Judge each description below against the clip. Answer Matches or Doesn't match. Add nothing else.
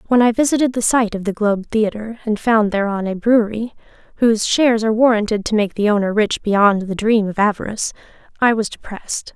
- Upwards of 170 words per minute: Matches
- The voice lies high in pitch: Matches